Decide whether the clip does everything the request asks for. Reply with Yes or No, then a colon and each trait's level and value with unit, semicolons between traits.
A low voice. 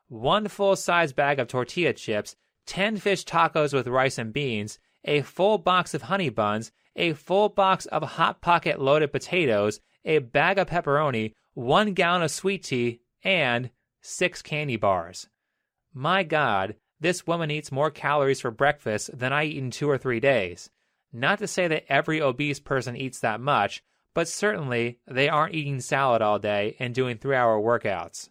No: medium, 145 Hz